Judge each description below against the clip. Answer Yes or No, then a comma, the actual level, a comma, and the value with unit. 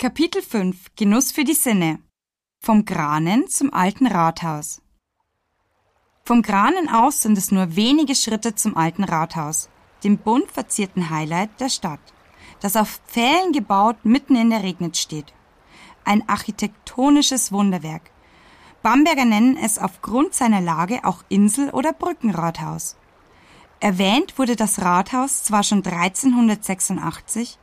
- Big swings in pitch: Yes, wide, 5.7 semitones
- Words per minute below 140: Yes, slow, 125 wpm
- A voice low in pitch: No, high, 215 Hz